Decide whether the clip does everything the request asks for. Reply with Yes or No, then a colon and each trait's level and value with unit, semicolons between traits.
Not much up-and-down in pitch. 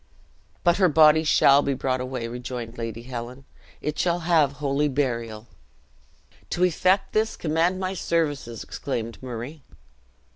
No: average, 5.1 semitones